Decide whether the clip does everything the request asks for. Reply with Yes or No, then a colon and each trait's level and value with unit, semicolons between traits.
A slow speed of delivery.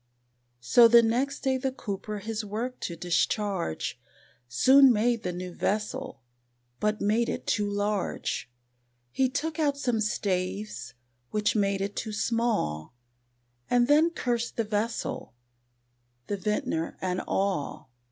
Yes: slow, 130 wpm